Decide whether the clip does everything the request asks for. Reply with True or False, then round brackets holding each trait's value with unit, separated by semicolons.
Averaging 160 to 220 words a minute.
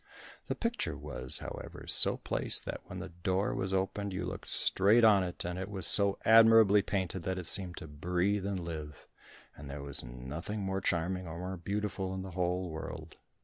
True (190 wpm)